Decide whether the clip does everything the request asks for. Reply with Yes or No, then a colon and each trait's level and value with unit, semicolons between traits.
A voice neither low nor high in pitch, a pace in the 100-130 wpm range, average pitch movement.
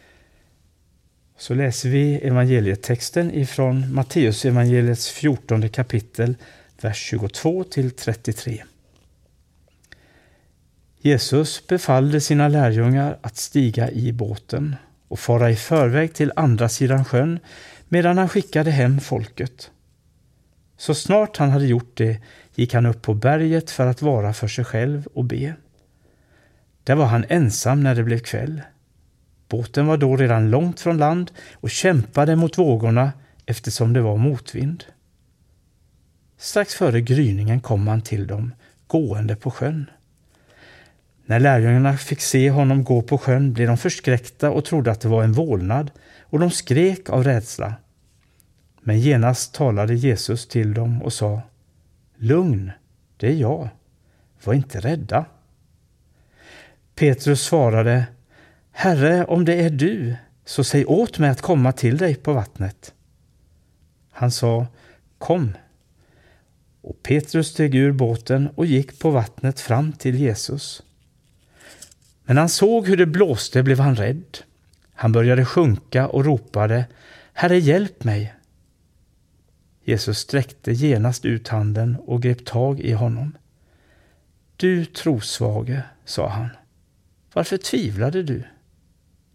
No: low, 125 Hz; slow, 125 wpm; average, 4.4 semitones